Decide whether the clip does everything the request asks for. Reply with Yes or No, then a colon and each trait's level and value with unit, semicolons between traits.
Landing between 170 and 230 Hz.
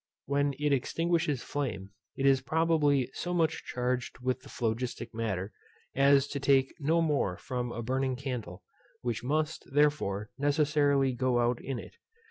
No: low, 135 Hz